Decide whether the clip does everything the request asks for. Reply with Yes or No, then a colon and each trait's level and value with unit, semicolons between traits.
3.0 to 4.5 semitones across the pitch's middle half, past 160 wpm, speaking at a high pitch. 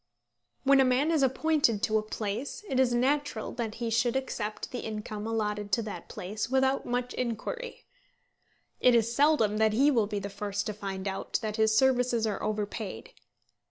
Yes: average, 3.7 semitones; average, 180 wpm; high, 225 Hz